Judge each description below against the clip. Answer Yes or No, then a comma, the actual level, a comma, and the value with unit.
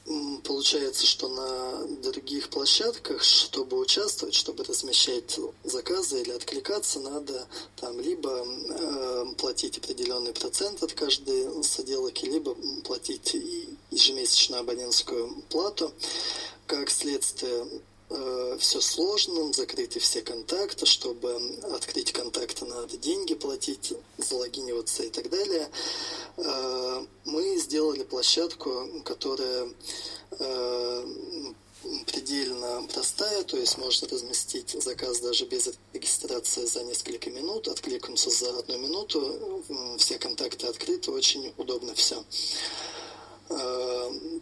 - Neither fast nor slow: No, slow, 95 wpm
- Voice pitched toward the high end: Yes, very high, 370 Hz